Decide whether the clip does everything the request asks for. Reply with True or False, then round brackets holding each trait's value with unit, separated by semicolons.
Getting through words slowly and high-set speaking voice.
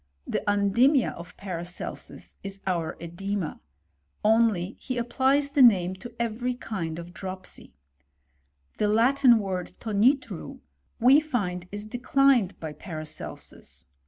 True (115 wpm; 205 Hz)